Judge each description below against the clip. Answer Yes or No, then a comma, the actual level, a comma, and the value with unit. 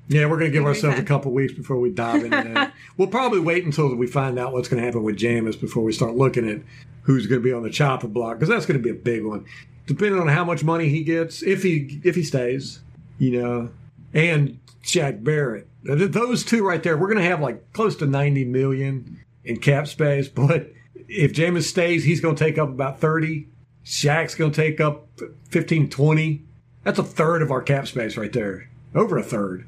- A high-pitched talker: No, medium, 140 Hz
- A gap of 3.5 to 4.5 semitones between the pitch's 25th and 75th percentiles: Yes, average, 4.2 semitones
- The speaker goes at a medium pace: No, fast, 225 wpm